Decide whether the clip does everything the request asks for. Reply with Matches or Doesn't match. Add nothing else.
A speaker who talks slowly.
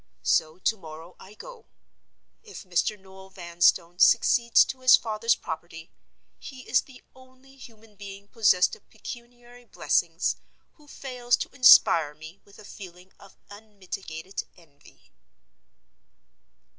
Matches